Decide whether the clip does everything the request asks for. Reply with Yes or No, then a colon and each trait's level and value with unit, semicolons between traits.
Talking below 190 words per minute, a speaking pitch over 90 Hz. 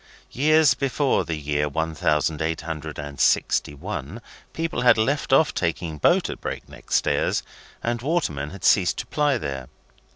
No: average, 165 wpm; very low, 85 Hz